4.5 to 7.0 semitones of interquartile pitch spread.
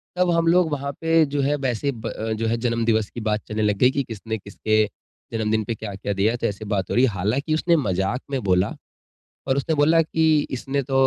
Yes: average, 5.2 semitones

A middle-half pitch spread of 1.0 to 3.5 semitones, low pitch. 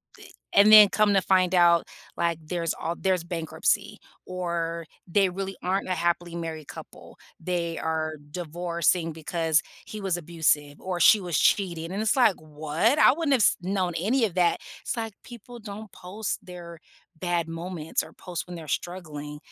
No: average, 2.8 semitones; medium, 175 Hz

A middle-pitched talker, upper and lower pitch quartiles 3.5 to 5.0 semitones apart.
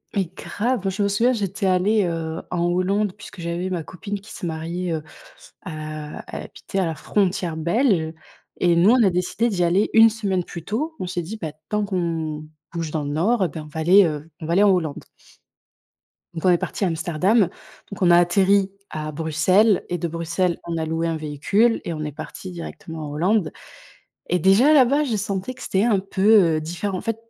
Yes: medium, 180 Hz; average, 3.8 semitones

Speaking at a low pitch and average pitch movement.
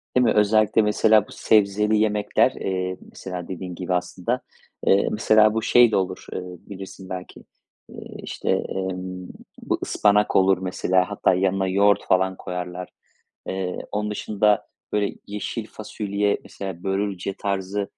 No: very low, 95 Hz; narrow, 2.2 semitones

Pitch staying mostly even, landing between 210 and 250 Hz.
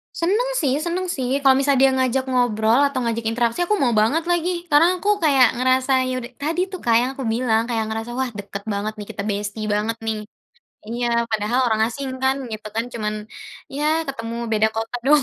No: average, 3.7 semitones; high, 245 Hz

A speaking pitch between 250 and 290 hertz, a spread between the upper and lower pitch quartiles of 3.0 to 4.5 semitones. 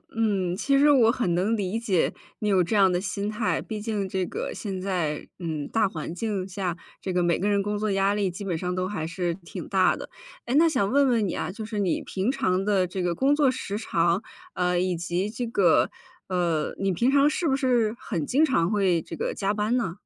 No: high, 195 Hz; average, 3.8 semitones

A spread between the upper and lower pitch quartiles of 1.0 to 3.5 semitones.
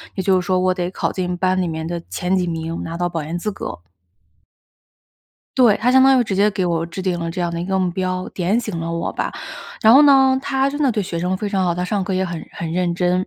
Yes: average, 2.9 semitones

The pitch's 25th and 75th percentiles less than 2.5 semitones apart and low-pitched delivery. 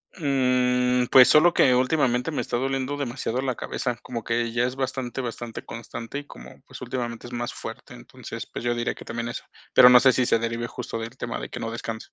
Yes: narrow, 1.8 semitones; low, 125 Hz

